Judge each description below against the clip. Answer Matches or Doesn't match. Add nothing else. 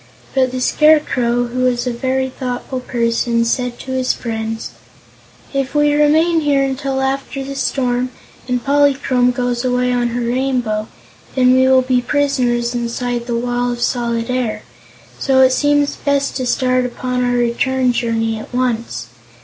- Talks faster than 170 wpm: Doesn't match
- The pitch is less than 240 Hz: Doesn't match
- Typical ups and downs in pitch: Doesn't match